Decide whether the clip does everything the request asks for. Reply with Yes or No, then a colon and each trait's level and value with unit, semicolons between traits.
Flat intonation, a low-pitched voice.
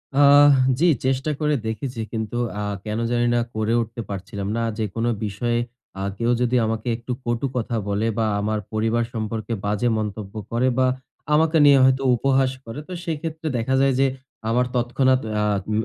No: average, 3.4 semitones; low, 120 Hz